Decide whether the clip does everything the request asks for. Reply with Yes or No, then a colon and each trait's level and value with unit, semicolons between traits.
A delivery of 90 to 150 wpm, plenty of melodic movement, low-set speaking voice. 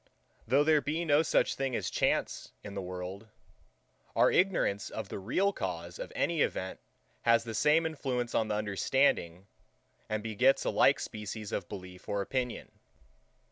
No: average, 160 wpm; wide, 6.1 semitones; low, 110 Hz